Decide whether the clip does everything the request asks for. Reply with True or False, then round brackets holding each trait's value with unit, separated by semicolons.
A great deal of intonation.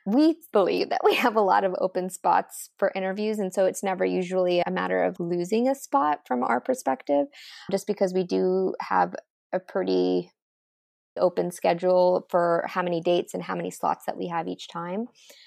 True (7.4 semitones)